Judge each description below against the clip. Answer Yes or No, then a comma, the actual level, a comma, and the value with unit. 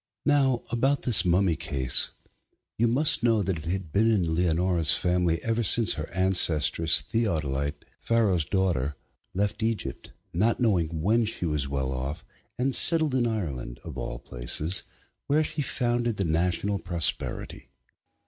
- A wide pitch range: Yes, wide, 6.3 semitones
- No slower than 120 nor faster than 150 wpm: Yes, average, 145 wpm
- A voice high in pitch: No, very low, 95 Hz